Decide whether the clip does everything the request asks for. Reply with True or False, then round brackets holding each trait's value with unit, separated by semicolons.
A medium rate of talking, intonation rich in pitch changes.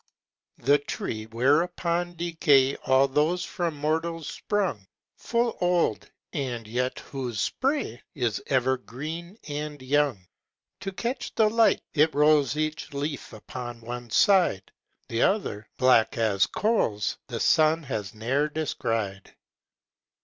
False (120 wpm; 5.7 semitones)